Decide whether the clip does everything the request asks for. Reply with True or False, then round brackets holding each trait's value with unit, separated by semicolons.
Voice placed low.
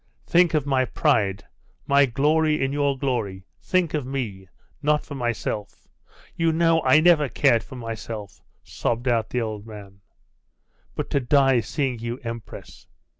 True (130 Hz)